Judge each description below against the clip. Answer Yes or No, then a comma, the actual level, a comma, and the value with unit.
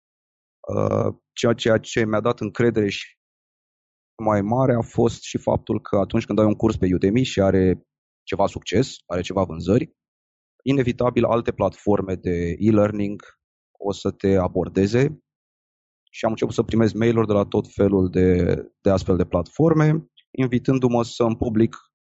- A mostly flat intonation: No, average, 4.0 semitones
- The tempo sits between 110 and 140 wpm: No, average, 150 wpm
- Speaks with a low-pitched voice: Yes, low, 105 Hz